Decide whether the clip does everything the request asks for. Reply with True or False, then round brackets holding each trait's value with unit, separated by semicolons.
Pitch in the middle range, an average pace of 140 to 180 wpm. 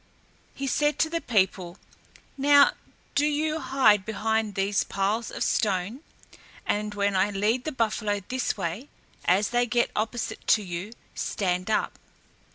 False (215 Hz; 145 wpm)